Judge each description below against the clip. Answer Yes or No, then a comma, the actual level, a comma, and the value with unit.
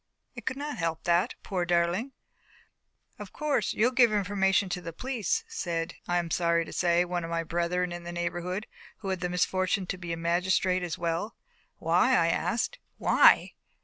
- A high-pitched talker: No, medium, 180 Hz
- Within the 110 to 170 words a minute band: No, average, 180 wpm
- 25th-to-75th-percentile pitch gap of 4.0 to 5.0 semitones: No, average, 2.9 semitones